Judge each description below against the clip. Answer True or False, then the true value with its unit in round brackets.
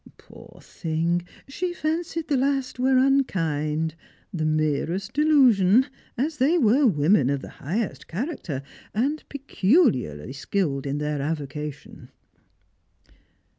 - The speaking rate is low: True (110 wpm)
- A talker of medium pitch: False (195 Hz)